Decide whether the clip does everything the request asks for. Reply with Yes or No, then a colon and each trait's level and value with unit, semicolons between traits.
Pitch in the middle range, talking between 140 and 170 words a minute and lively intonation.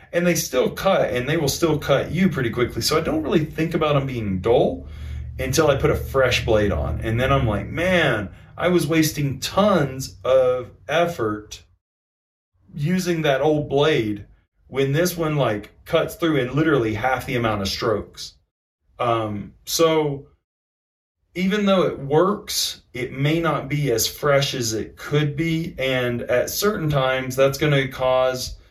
No: low, 130 Hz; average, 165 wpm; wide, 6.8 semitones